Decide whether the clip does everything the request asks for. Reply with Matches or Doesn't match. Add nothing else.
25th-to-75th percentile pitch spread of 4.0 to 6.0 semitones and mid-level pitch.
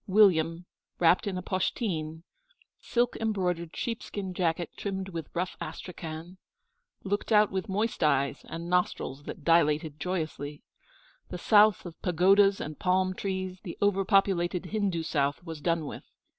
Doesn't match